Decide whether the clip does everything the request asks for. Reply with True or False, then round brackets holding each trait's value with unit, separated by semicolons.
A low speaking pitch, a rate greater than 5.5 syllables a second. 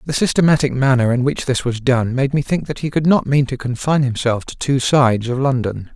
True (130 Hz; 5.7 syllables/s)